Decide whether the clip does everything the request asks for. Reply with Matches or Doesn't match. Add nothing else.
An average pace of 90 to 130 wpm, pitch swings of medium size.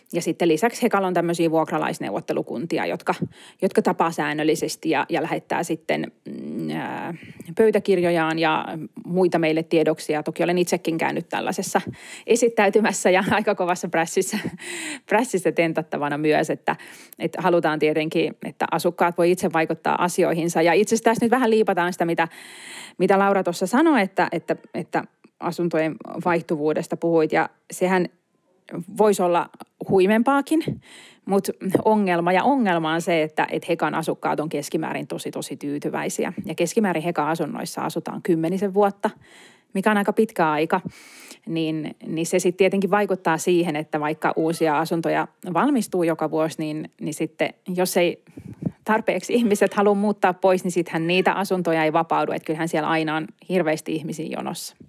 Doesn't match